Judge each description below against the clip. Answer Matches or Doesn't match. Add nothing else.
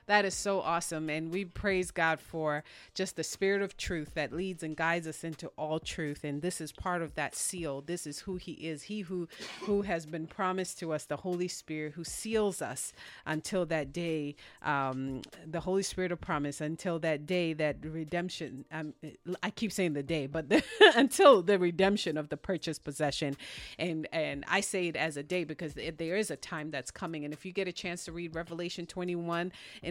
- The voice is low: Doesn't match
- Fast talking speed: Matches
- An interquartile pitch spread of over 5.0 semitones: Doesn't match